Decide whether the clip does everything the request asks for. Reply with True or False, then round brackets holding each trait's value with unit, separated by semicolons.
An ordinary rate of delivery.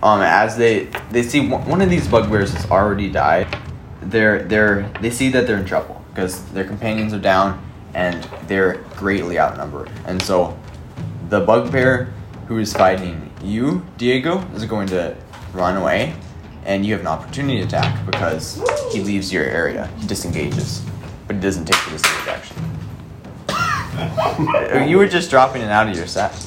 True (165 wpm)